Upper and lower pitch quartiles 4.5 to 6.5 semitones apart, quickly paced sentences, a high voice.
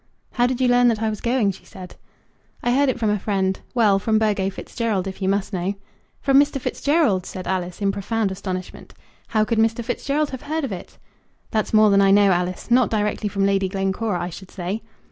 No: average, 3.6 semitones; fast, 220 wpm; high, 210 Hz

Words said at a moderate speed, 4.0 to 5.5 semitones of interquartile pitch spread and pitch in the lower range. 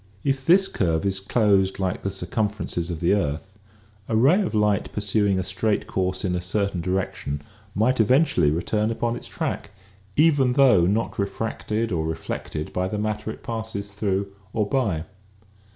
No: average, 165 wpm; average, 3.3 semitones; low, 100 Hz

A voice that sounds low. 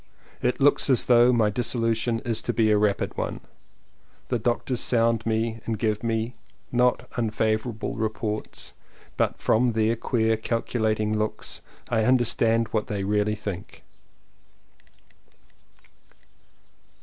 Yes: low, 115 Hz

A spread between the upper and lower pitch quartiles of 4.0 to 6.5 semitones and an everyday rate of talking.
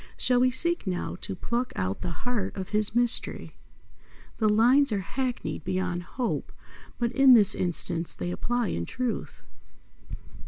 Yes: average, 5.2 semitones; average, 150 wpm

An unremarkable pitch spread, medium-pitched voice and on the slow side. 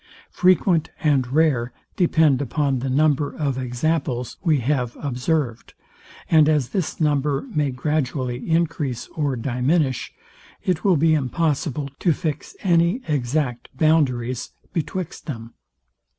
Yes: average, 4.0 semitones; medium, 145 Hz; slow, 120 wpm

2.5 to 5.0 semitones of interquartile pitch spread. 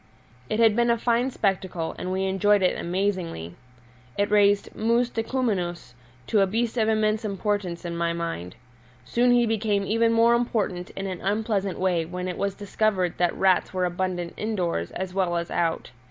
Yes: average, 3.7 semitones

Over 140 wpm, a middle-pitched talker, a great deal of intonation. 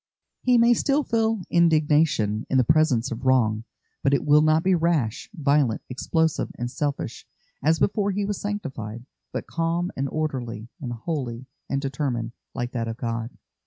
Yes: average, 160 wpm; medium, 145 Hz; wide, 5.7 semitones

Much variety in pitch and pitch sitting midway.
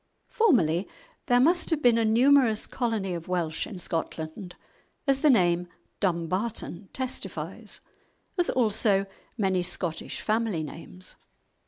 No: wide, 5.7 semitones; high, 205 Hz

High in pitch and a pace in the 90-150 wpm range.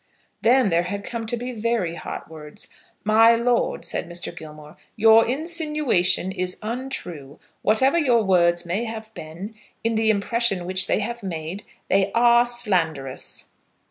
Yes: high, 215 Hz; average, 145 wpm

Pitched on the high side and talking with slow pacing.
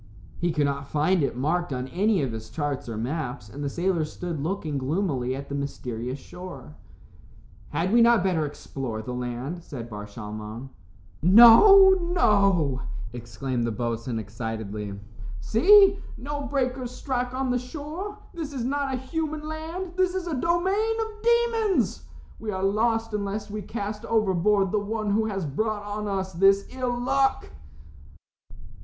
No: high, 195 Hz; average, 155 wpm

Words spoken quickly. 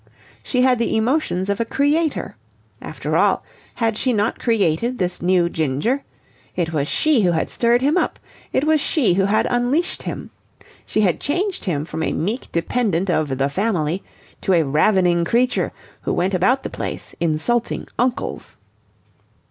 No: average, 165 wpm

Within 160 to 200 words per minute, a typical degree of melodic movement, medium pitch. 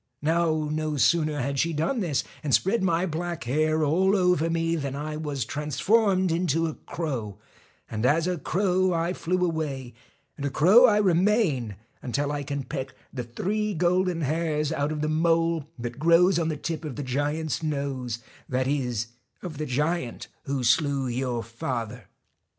Yes: average, 170 wpm; average, 3.7 semitones; medium, 155 Hz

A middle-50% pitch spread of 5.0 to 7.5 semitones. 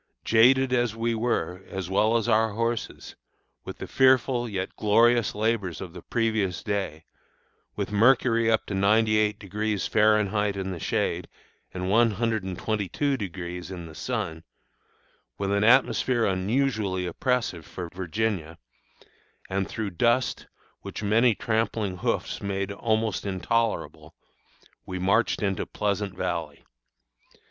No: average, 3.4 semitones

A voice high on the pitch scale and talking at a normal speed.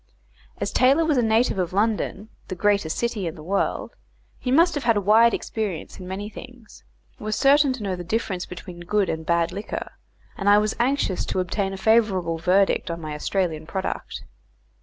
Yes: high, 200 Hz; average, 190 wpm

